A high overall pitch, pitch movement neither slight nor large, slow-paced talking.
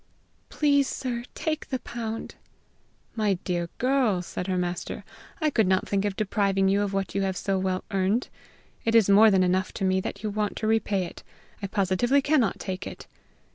No: high, 200 Hz; average, 3.3 semitones; average, 190 wpm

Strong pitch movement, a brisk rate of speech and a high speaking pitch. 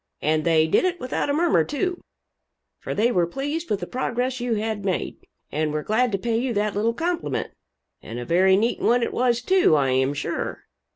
Yes: wide, 7.1 semitones; fast, 210 wpm; high, 225 Hz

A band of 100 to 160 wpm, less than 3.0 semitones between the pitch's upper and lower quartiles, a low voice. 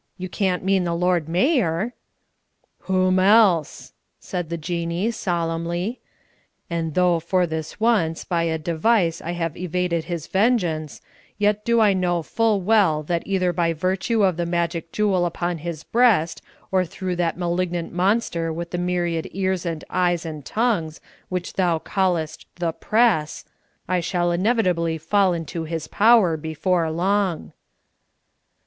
No: average, 145 wpm; narrow, 2.5 semitones; medium, 175 Hz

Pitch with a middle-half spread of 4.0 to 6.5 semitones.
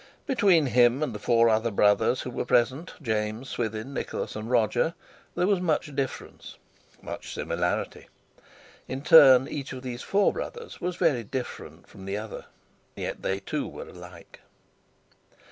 Yes: average, 5.2 semitones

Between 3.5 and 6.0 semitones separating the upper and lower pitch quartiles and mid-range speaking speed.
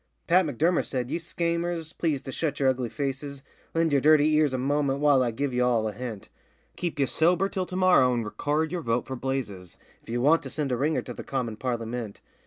No: average, 4.3 semitones; fast, 225 wpm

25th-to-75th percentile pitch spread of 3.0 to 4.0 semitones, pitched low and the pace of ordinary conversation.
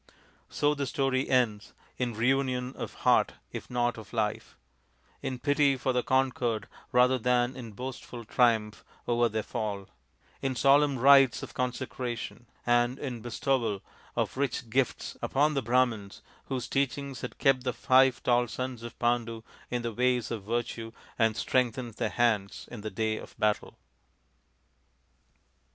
No: narrow, 2.4 semitones; low, 125 Hz; average, 145 wpm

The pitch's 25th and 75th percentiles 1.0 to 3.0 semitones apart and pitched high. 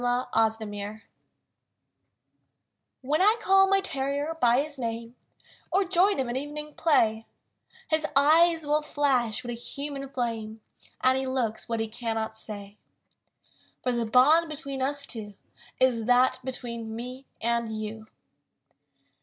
No: average, 4.5 semitones; very high, 250 Hz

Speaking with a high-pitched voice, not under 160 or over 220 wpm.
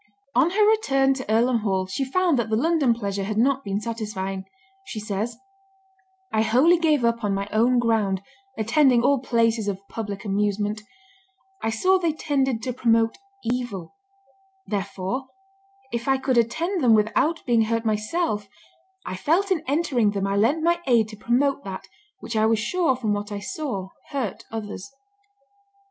Yes: high, 230 Hz; average, 165 wpm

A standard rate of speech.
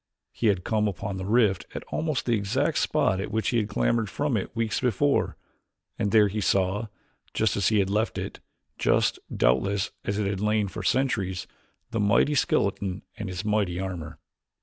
Yes: average, 185 wpm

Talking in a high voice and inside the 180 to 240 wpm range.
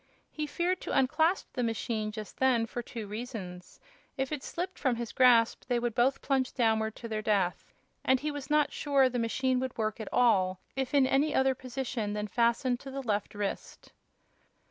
Yes: high, 245 Hz; average, 190 wpm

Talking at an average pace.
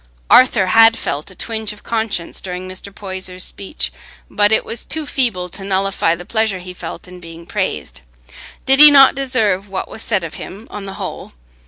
Yes: average, 190 wpm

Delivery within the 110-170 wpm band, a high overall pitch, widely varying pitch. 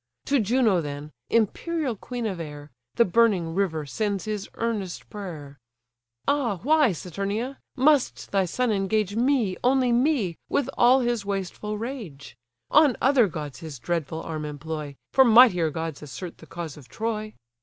Yes: average, 150 wpm; high, 205 Hz; wide, 6.8 semitones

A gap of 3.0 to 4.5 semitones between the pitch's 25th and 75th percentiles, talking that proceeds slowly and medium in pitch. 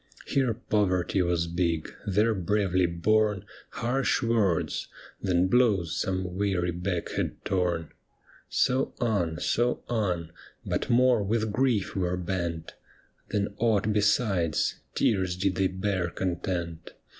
No: average, 3.6 semitones; slow, 120 wpm; very low, 95 Hz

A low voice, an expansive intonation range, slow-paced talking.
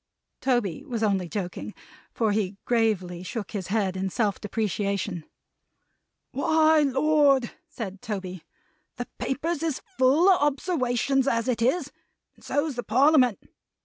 No: high, 235 Hz; wide, 5.7 semitones; slow, 130 wpm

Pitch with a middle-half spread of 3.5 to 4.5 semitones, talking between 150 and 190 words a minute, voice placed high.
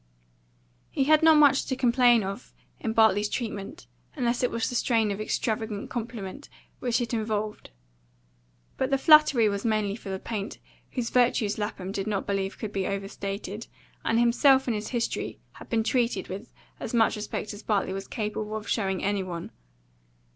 No: average, 3.1 semitones; average, 170 wpm; high, 220 Hz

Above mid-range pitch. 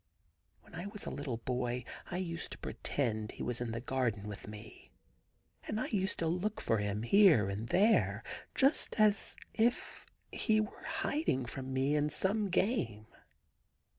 No: medium, 140 Hz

